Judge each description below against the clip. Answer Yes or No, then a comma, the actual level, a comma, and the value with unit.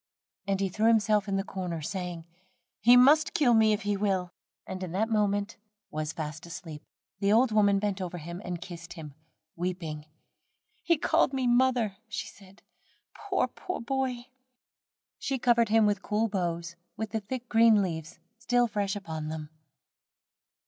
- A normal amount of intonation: Yes, average, 4.5 semitones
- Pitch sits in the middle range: No, high, 200 Hz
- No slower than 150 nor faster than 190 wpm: Yes, average, 165 wpm